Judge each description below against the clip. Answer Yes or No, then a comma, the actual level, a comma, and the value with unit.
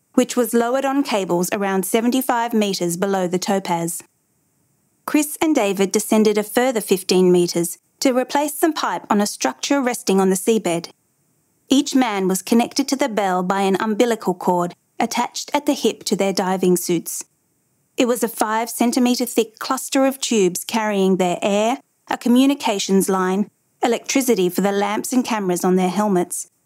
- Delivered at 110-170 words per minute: Yes, average, 165 wpm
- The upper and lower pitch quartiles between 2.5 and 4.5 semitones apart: No, average, 5.0 semitones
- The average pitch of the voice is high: Yes, high, 215 Hz